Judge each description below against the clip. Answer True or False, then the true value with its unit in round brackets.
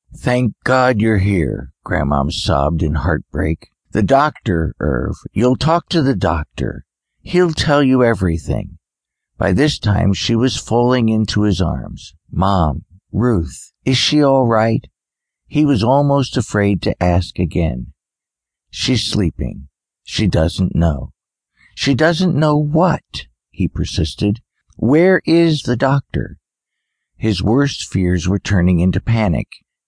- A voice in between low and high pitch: False (105 Hz)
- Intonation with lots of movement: True (7.2 semitones)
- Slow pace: True (125 wpm)